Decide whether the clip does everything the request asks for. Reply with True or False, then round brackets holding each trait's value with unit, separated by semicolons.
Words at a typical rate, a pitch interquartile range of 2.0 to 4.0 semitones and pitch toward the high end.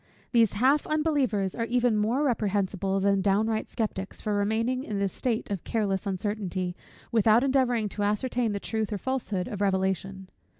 True (160 wpm; 3.4 semitones; 210 Hz)